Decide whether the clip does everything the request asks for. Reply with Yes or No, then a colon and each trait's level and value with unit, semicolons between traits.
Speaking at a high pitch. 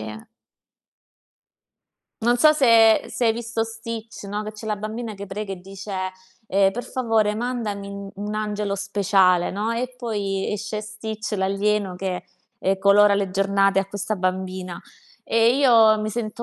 Yes: high, 210 Hz